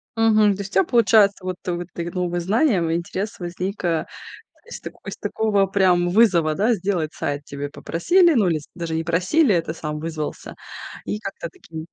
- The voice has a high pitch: No, medium, 180 Hz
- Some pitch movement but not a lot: Yes, average, 3.9 semitones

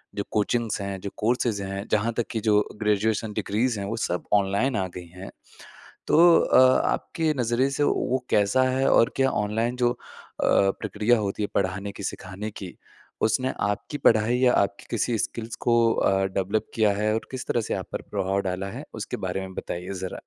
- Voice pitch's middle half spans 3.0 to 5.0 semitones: Yes, average, 3.5 semitones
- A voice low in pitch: Yes, low, 110 Hz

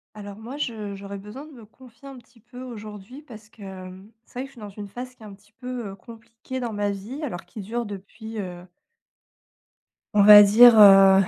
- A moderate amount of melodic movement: Yes, average, 3.4 semitones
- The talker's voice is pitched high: Yes, high, 215 Hz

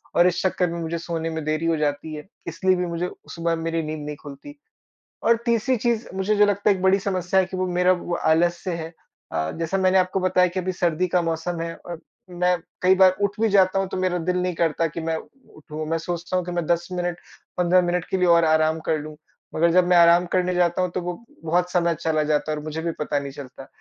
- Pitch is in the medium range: Yes, medium, 175 Hz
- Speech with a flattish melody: Yes, narrow, 2.2 semitones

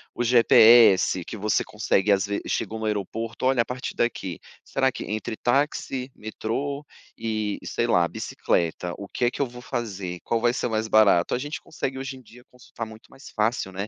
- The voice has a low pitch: Yes, low, 115 Hz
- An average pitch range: Yes, average, 3.1 semitones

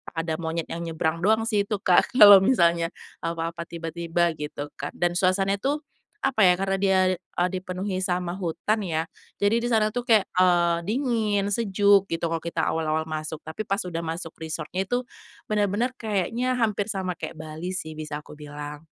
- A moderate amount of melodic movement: Yes, average, 3.7 semitones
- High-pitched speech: No, medium, 180 Hz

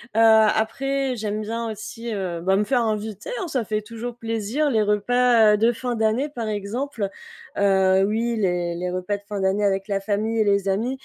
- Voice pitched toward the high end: Yes, high, 215 Hz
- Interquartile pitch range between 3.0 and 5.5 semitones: No, narrow, 2.6 semitones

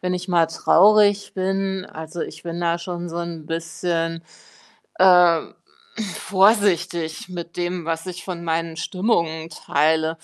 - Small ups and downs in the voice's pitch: Yes, narrow, 2.1 semitones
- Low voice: No, medium, 170 Hz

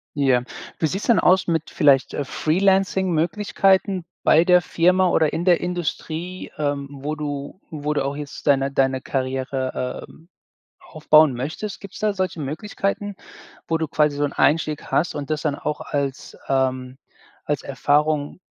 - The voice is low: No, medium, 155 Hz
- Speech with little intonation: No, average, 4.2 semitones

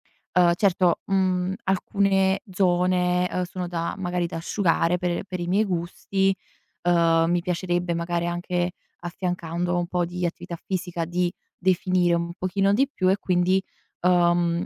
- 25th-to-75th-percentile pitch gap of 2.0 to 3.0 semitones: No, narrow, 1.3 semitones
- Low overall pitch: No, medium, 180 Hz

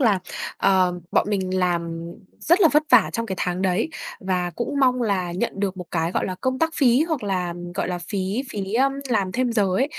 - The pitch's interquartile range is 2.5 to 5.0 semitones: No, wide, 5.4 semitones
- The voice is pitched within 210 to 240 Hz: No, high, 195 Hz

